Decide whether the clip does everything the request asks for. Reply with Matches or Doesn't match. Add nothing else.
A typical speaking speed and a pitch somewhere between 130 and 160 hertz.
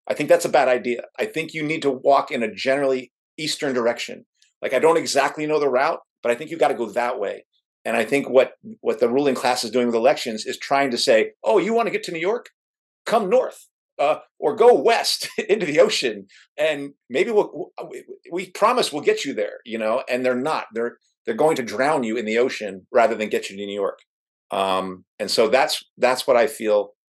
Doesn't match